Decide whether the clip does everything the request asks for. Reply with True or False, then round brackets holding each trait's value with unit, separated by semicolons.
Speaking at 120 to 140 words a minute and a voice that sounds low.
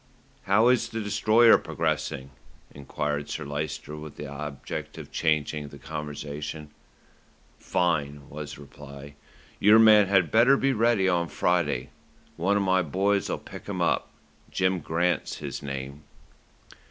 True (135 wpm; 80 Hz)